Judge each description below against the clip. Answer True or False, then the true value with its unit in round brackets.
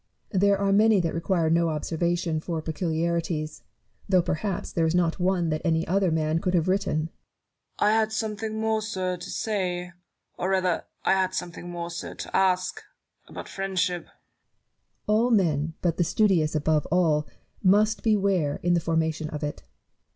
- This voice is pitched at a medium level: True (175 Hz)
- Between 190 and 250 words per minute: False (180 wpm)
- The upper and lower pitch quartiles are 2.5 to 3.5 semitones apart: True (3.1 semitones)